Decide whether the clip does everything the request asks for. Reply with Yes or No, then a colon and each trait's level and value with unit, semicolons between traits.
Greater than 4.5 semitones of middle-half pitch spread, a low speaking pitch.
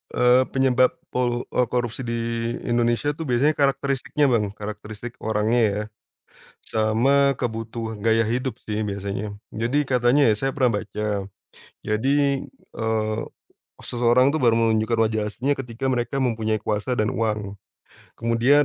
No: average, 2.9 semitones; low, 120 Hz